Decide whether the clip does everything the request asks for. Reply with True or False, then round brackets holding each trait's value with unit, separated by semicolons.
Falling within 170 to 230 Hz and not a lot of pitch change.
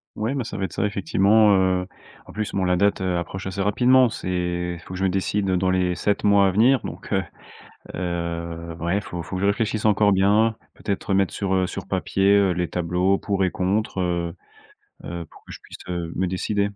False (95 Hz; 2.3 semitones)